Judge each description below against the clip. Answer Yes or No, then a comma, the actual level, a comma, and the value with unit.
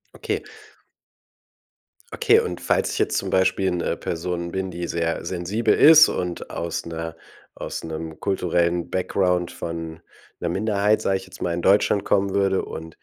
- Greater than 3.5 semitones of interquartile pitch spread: No, narrow, 2.4 semitones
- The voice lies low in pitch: Yes, very low, 90 Hz